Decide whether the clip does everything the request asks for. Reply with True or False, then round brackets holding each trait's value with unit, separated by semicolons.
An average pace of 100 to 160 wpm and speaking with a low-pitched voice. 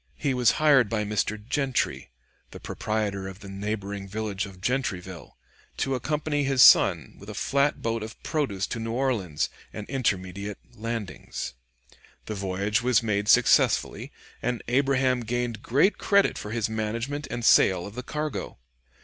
True (150 wpm; 110 Hz)